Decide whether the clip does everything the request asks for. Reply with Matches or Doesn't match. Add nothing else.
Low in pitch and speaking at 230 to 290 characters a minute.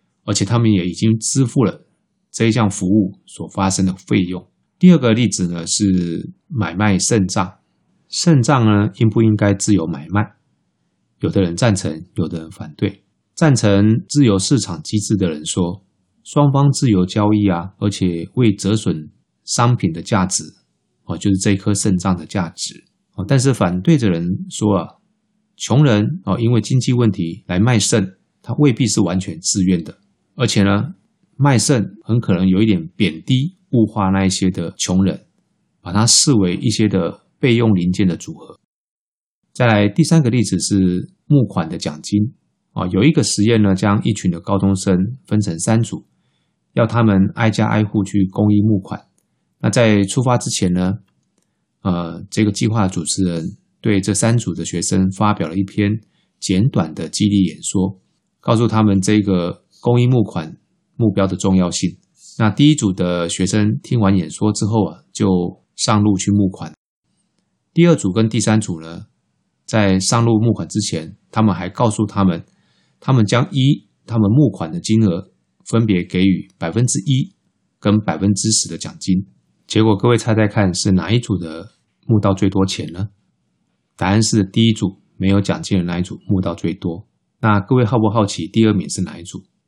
Matches